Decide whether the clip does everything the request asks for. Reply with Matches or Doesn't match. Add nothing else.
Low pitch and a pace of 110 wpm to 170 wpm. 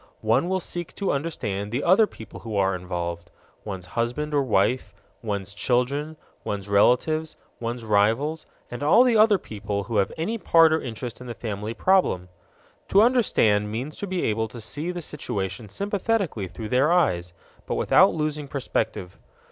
Matches